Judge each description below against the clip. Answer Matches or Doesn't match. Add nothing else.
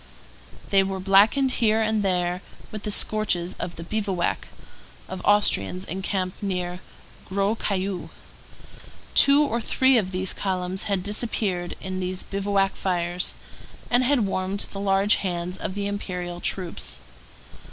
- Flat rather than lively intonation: Matches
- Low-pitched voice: Doesn't match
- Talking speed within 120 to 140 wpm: Matches